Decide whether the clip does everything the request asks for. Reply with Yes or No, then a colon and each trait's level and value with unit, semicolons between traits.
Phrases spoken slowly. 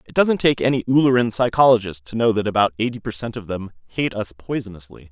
No: average, 200 wpm